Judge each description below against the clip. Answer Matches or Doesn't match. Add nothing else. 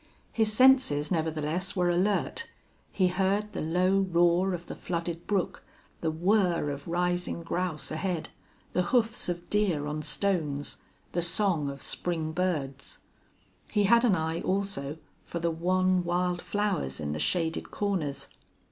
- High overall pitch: Doesn't match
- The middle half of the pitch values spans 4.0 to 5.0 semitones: Doesn't match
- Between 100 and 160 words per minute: Matches